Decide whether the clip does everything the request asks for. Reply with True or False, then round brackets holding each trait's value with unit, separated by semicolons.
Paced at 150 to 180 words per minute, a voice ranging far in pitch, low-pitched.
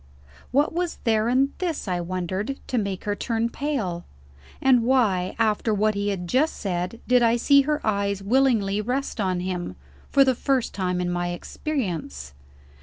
False (170 wpm; 6.0 semitones; 215 Hz)